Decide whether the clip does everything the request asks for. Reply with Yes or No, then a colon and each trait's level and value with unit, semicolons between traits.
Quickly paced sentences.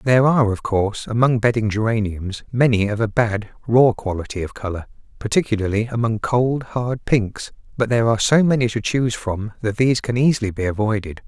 No: average, 180 wpm